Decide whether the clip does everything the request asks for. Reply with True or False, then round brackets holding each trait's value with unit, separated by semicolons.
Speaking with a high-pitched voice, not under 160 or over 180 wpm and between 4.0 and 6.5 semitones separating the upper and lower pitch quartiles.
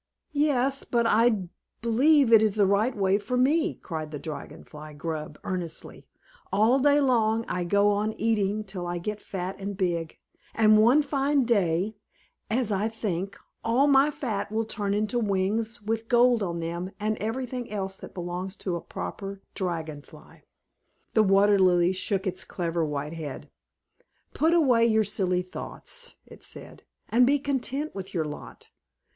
True (210 Hz; 165 wpm; 4.6 semitones)